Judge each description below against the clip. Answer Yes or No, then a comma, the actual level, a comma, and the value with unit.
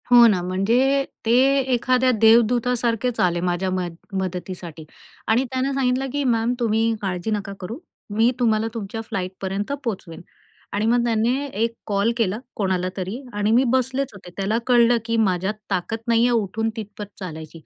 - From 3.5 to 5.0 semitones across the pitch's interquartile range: Yes, average, 4.1 semitones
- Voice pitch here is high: Yes, high, 220 Hz